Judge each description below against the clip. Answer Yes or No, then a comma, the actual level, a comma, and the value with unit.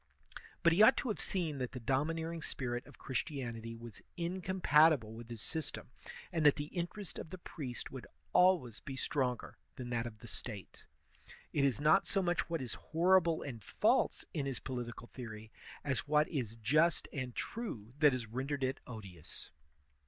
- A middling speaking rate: Yes, average, 175 wpm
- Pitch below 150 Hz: Yes, low, 135 Hz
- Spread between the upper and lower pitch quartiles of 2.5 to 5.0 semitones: No, wide, 5.6 semitones